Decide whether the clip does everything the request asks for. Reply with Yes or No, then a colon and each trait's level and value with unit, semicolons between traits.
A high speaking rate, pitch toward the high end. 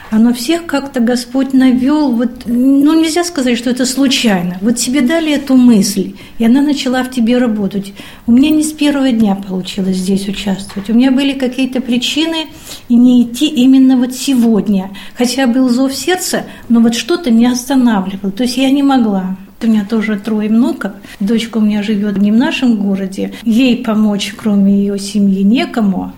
Yes: fast, 180 wpm; high, 240 Hz